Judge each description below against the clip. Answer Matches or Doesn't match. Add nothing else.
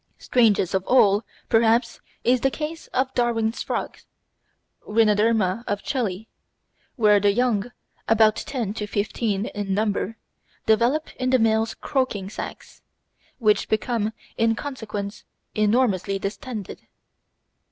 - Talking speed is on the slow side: Matches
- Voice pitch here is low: Doesn't match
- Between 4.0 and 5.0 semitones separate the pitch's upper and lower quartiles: Doesn't match